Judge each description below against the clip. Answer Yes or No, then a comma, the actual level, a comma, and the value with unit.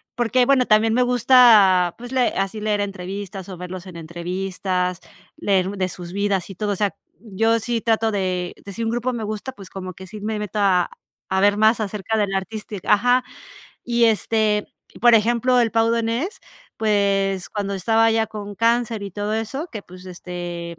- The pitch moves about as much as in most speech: Yes, average, 3.1 semitones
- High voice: Yes, high, 210 Hz